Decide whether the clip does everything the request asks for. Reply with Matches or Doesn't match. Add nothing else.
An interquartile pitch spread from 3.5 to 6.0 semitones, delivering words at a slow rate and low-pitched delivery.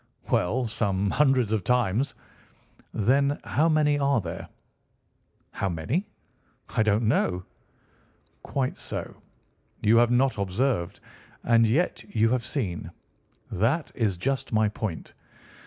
Matches